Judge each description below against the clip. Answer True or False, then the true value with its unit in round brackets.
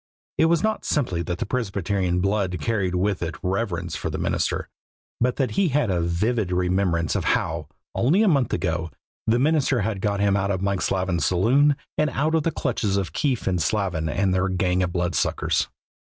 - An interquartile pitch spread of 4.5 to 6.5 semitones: True (5.5 semitones)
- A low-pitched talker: True (95 Hz)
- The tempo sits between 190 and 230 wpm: True (195 wpm)